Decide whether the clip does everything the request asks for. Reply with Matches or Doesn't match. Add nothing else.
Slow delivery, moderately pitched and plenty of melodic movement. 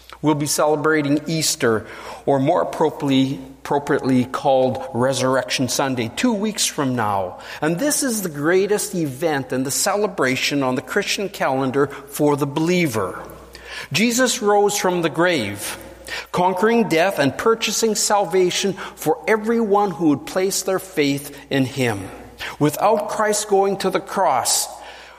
Matches